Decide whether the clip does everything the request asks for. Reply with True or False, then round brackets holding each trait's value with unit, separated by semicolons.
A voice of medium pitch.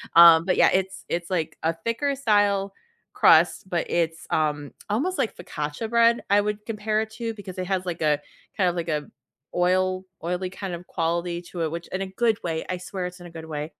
True (180 Hz)